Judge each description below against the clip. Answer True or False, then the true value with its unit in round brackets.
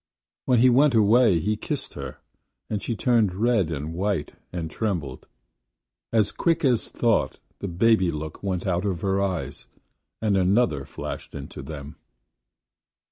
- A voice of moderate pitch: False (100 Hz)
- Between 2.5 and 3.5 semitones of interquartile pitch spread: False (5.0 semitones)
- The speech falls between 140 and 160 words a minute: True (145 wpm)